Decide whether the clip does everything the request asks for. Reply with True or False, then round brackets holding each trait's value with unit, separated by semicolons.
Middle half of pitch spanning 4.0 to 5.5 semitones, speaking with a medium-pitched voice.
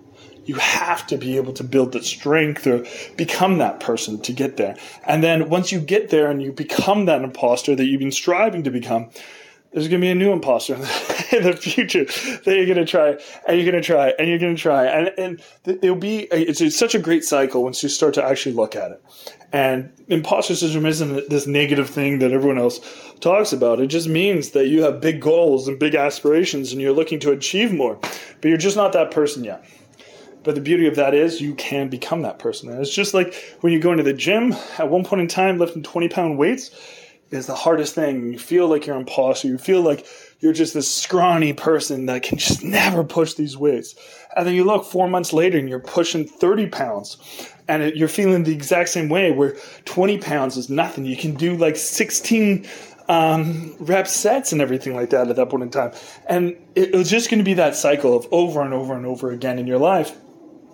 True (4.6 semitones; 160 Hz)